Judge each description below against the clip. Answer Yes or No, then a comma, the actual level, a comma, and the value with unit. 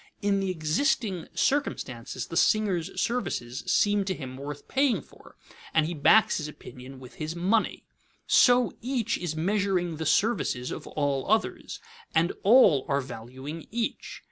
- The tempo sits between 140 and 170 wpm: Yes, average, 145 wpm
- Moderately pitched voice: Yes, medium, 175 Hz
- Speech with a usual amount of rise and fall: No, wide, 7.1 semitones